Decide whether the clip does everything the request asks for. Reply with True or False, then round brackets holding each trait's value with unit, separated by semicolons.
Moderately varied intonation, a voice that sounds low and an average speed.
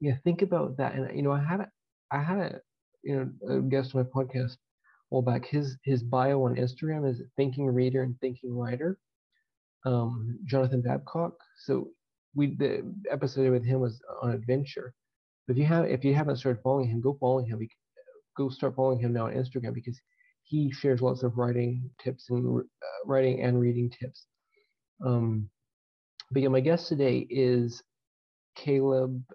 False (2.0 semitones; 130 Hz; 180 wpm)